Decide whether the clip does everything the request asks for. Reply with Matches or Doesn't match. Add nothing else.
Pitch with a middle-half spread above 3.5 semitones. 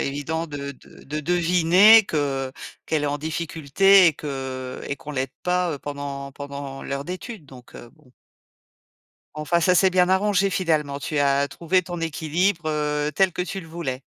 Matches